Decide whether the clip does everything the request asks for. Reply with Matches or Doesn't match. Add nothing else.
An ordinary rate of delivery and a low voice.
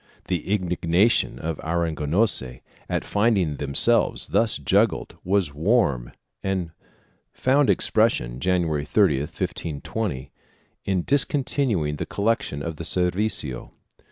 Doesn't match